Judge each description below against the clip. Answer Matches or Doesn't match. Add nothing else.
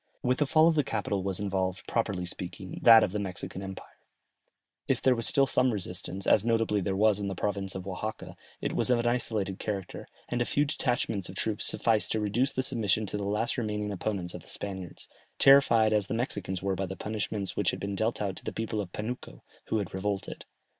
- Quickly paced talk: Matches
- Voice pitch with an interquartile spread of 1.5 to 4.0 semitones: Matches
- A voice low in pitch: Matches